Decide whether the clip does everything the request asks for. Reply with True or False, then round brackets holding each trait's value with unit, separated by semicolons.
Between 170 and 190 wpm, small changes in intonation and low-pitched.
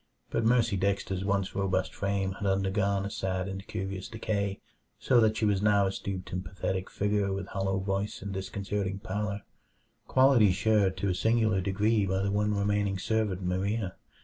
True (175 wpm; 1.5 semitones; 100 Hz)